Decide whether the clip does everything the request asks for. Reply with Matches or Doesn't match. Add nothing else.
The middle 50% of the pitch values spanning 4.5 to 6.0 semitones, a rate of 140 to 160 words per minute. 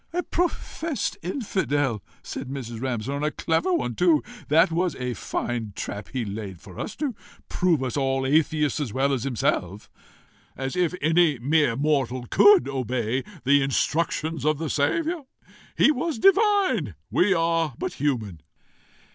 Matches